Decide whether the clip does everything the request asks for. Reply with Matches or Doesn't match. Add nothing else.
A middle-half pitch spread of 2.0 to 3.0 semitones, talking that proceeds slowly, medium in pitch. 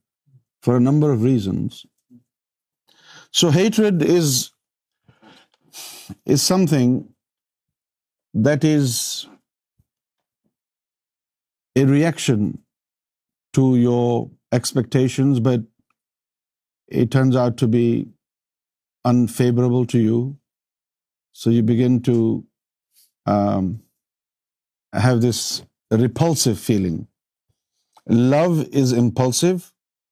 Doesn't match